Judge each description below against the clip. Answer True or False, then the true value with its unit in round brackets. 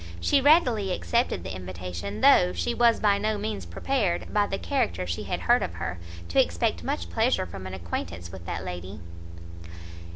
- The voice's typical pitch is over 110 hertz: False (95 Hz)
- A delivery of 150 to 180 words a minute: True (175 wpm)